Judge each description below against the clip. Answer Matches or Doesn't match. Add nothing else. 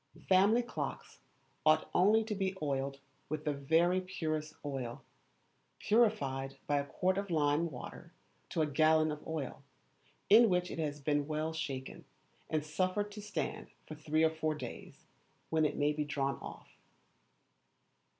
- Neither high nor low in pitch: Matches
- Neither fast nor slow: Matches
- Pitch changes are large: Doesn't match